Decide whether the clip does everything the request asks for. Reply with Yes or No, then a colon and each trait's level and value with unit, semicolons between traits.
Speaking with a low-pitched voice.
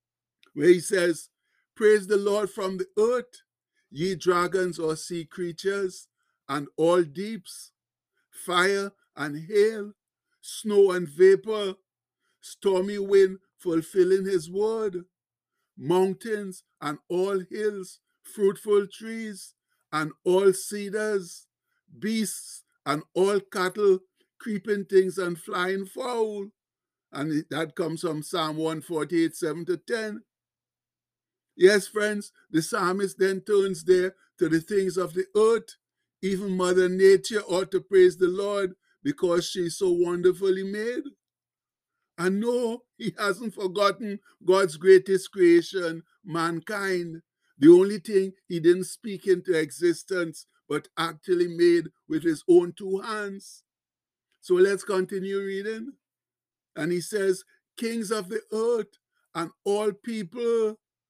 No: high, 195 Hz